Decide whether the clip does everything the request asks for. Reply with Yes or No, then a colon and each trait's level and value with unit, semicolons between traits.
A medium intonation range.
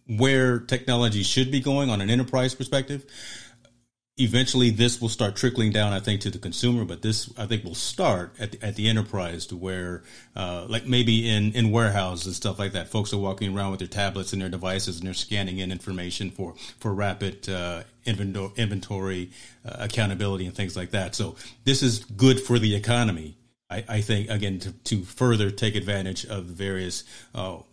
Yes: average, 3.9 semitones